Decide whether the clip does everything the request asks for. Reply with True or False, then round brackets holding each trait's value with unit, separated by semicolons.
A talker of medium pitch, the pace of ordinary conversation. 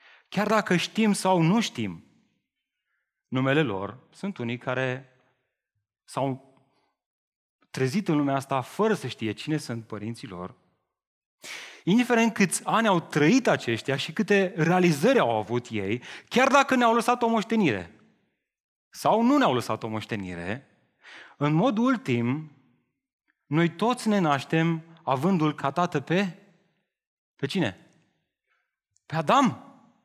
True (155 Hz; 125 wpm)